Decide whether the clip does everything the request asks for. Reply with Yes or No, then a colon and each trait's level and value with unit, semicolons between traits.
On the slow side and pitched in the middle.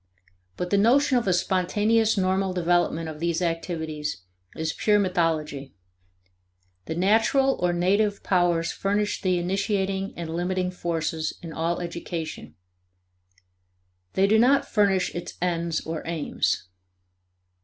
Yes: slow, 120 wpm; medium, 180 Hz